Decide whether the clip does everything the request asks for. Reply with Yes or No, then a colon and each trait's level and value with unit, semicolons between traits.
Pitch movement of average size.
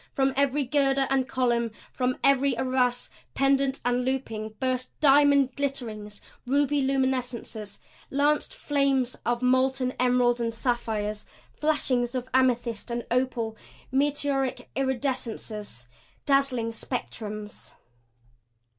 No: narrow, 2.3 semitones